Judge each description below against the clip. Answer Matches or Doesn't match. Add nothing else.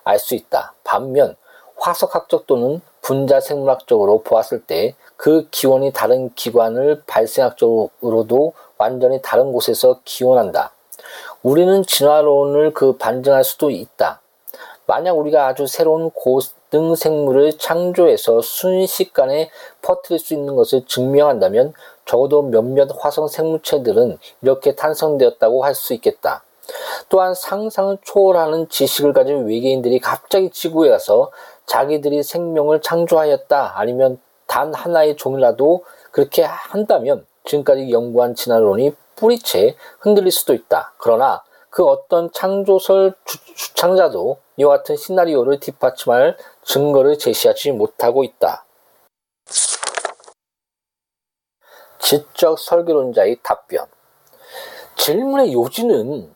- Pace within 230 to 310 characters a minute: Matches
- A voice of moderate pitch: Matches